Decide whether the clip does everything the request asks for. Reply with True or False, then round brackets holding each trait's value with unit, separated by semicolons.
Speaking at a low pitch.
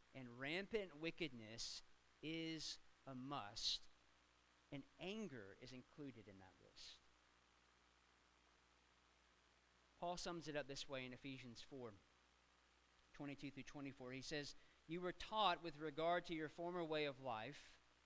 True (125 Hz)